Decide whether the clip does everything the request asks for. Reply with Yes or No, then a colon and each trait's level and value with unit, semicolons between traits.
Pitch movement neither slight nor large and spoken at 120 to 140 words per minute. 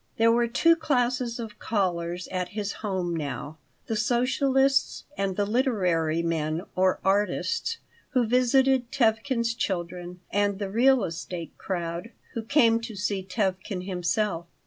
Yes: average, 4.9 semitones; slow, 135 wpm